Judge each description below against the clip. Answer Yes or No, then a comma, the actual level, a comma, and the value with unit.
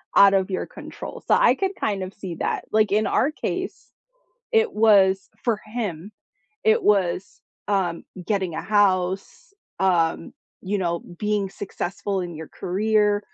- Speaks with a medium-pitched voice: No, high, 200 Hz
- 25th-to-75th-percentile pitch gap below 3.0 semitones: Yes, narrow, 2.4 semitones